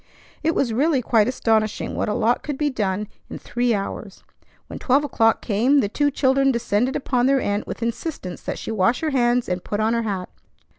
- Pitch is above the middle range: Yes, high, 235 Hz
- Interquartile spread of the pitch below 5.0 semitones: Yes, average, 4.0 semitones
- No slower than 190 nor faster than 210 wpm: Yes, fast, 205 wpm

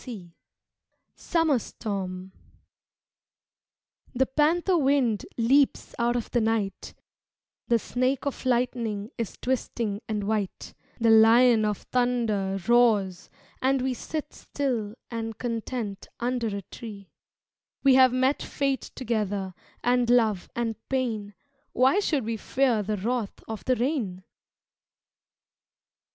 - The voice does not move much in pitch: No, average, 3.4 semitones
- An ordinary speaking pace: No, slow, 115 wpm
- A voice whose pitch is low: No, high, 235 Hz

